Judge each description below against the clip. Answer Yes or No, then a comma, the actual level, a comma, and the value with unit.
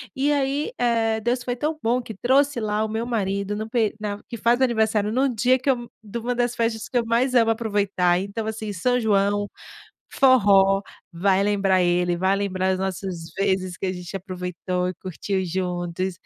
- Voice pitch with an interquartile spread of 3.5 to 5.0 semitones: Yes, average, 4.0 semitones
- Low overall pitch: No, high, 210 Hz